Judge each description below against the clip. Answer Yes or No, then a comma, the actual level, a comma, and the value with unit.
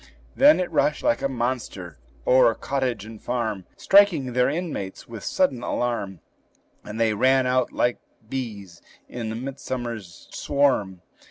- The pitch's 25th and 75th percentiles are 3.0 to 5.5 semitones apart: Yes, average, 3.6 semitones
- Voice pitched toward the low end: Yes, low, 120 Hz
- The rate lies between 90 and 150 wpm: Yes, average, 140 wpm